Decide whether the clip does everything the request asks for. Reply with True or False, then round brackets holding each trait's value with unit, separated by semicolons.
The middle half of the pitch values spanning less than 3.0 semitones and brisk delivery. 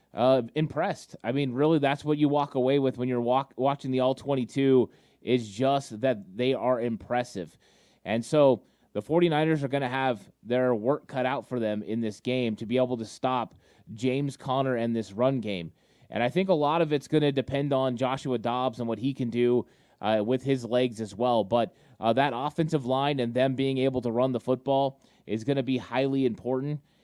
True (2.4 semitones; 210 wpm)